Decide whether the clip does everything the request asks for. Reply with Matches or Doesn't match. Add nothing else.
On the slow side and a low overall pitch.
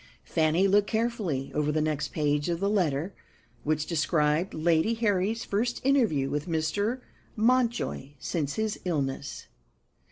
Doesn't match